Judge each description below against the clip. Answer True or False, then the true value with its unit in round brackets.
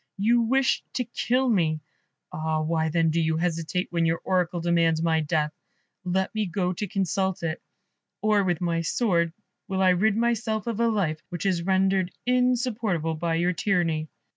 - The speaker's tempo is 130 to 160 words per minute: False (170 wpm)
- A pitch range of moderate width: True (4.2 semitones)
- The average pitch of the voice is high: False (180 Hz)